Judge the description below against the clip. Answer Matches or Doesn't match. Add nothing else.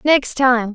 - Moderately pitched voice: Doesn't match